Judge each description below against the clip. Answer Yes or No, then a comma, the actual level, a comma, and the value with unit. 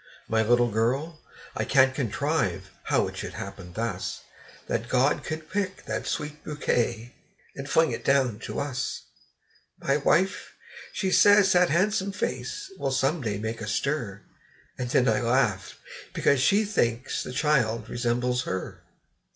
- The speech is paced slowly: No, average, 150 wpm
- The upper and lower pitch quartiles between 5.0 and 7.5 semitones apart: Yes, average, 5.3 semitones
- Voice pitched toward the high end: No, low, 130 Hz